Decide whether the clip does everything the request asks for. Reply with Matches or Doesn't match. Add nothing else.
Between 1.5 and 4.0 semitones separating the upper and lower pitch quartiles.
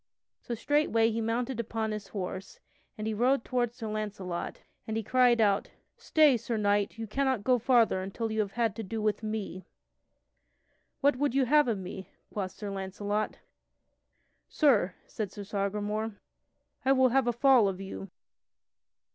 Matches